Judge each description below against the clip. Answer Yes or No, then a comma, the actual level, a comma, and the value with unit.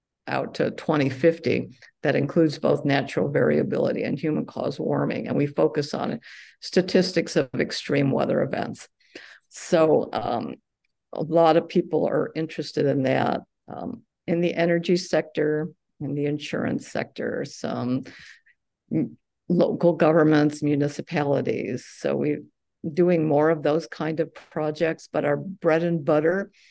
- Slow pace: Yes, slow, 130 wpm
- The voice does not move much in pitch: Yes, narrow, 2.2 semitones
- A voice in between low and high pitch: Yes, medium, 160 Hz